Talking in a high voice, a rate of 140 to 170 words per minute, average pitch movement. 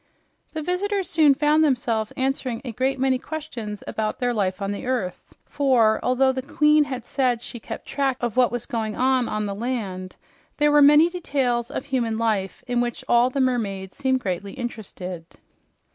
No: very high, 250 Hz; average, 180 wpm; average, 3.8 semitones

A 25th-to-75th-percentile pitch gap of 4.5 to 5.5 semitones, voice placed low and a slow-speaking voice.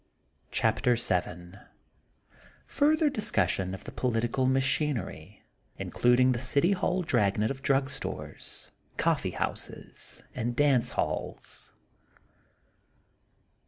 Yes: average, 4.9 semitones; low, 125 Hz; slow, 95 wpm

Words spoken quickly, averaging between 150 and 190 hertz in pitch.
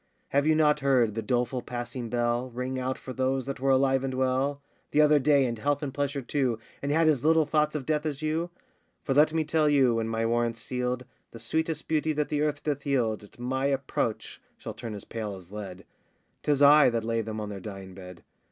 No: fast, 225 wpm; low, 130 Hz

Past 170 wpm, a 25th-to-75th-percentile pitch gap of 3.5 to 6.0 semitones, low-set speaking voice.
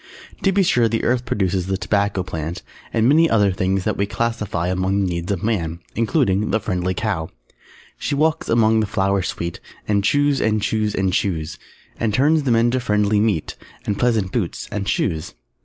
Yes: average, 190 wpm; average, 3.8 semitones; low, 105 Hz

